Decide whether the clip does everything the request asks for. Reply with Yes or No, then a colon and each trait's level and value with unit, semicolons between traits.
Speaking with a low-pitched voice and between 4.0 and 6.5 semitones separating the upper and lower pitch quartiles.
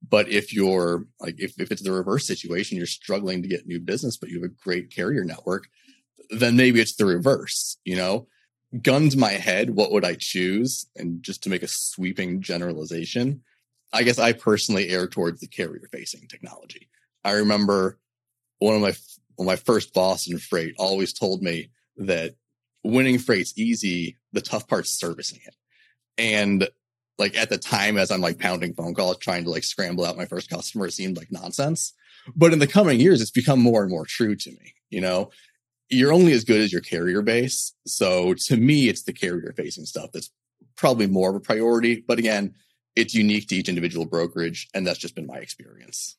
Yes: low, 105 Hz; average, 5.2 semitones